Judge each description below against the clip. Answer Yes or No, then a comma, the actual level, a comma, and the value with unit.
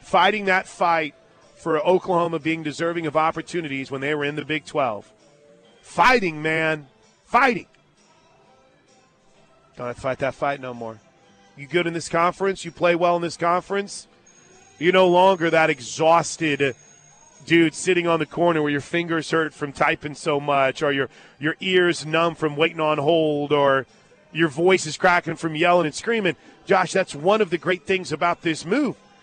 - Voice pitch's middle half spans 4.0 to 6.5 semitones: No, average, 2.9 semitones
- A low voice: No, medium, 165 Hz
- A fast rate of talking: No, average, 170 wpm